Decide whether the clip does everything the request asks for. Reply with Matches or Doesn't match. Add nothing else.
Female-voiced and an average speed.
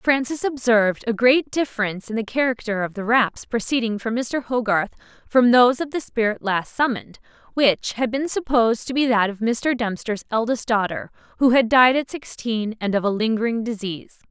Matches